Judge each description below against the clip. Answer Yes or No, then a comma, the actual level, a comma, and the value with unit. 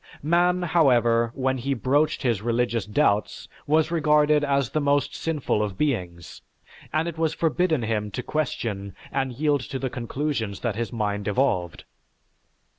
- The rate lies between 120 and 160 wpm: Yes, average, 150 wpm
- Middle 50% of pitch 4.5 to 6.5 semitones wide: Yes, average, 5.2 semitones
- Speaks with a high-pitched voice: No, low, 130 Hz